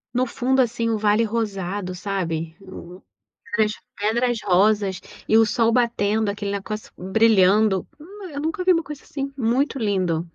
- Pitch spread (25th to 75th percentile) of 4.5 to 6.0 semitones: No, average, 3.9 semitones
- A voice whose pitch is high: Yes, high, 215 Hz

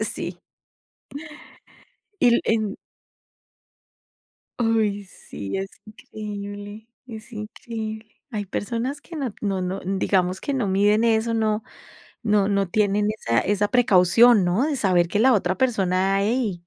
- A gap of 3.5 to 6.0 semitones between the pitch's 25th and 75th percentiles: No, average, 2.7 semitones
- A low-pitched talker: No, high, 210 Hz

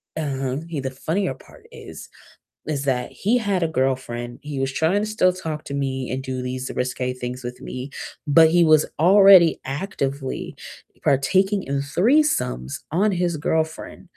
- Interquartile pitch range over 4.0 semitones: Yes, average, 5.2 semitones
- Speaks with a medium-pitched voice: Yes, medium, 145 Hz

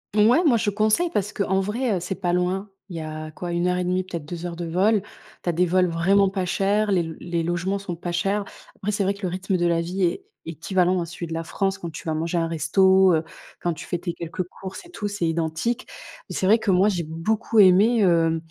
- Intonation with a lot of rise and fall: No, average, 2.8 semitones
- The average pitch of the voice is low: No, medium, 180 Hz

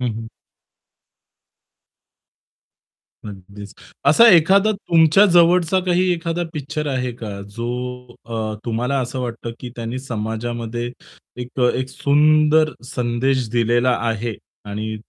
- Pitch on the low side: Yes, low, 125 Hz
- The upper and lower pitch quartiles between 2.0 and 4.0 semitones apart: No, average, 5.0 semitones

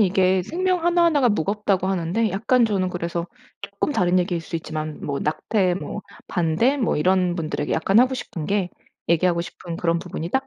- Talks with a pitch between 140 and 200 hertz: Yes, medium, 185 Hz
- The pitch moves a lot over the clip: No, average, 4.4 semitones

